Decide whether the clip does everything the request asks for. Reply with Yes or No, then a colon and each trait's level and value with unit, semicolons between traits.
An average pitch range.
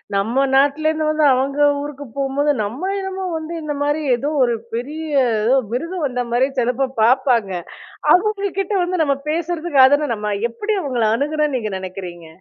Yes: average, 4.2 semitones